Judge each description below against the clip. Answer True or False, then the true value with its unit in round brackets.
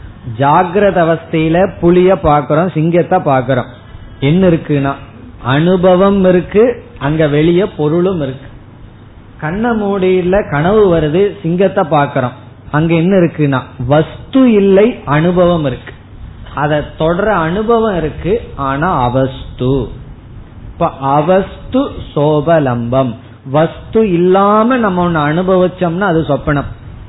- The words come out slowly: False (95 wpm)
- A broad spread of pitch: True (5.8 semitones)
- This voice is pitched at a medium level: True (155 Hz)